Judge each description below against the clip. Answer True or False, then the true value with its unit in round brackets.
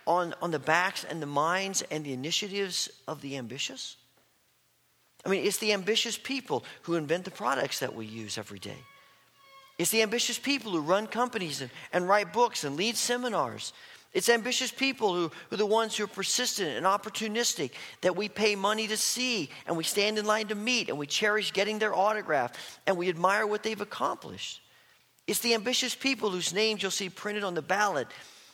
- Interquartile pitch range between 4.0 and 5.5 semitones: True (4.6 semitones)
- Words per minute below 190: False (195 wpm)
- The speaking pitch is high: True (205 Hz)